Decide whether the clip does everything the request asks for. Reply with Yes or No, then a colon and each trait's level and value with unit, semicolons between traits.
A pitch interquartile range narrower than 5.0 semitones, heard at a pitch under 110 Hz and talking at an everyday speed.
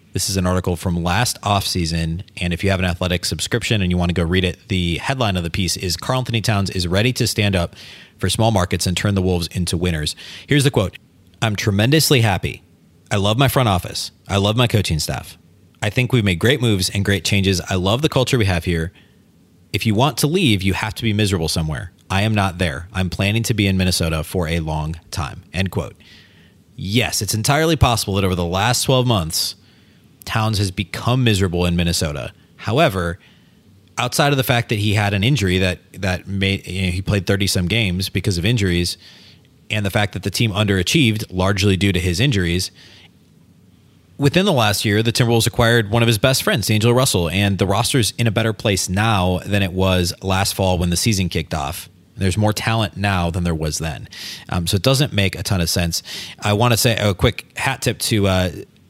No: average, 3.9 semitones; low, 100 Hz; fast, 215 wpm